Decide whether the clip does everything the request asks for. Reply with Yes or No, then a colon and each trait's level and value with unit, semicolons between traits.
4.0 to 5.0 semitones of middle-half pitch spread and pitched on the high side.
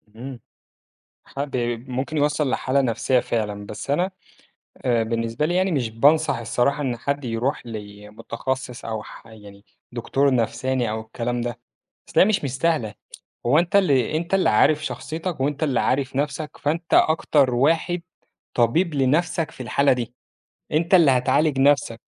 No: average, 4.7 semitones; low, 135 Hz